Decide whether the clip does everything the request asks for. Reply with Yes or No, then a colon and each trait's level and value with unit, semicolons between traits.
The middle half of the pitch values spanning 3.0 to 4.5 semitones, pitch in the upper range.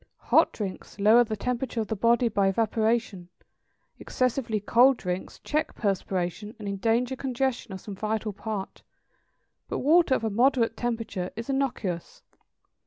Yes: average, 3.6 semitones; high, 225 Hz